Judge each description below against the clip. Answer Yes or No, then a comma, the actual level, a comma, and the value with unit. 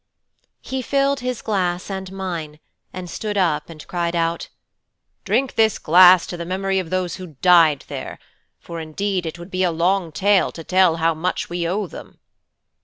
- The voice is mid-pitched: Yes, medium, 180 Hz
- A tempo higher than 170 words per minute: Yes, average, 180 wpm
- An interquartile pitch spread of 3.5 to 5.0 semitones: No, narrow, 2.6 semitones